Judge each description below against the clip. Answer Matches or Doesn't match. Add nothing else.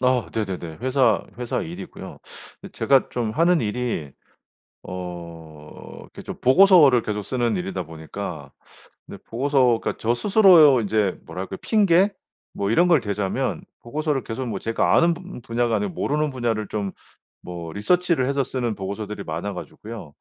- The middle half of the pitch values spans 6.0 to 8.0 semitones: Matches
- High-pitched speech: Doesn't match